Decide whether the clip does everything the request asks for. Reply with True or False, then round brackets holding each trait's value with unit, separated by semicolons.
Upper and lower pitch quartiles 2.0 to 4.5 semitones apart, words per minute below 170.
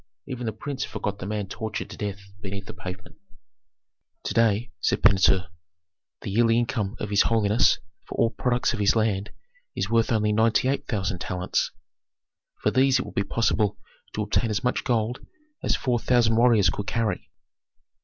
False (2.8 semitones; 175 wpm)